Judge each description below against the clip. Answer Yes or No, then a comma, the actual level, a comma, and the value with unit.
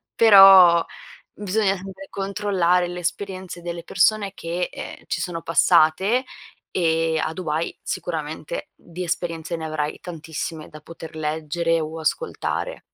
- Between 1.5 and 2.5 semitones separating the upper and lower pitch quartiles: No, average, 2.9 semitones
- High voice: No, medium, 170 Hz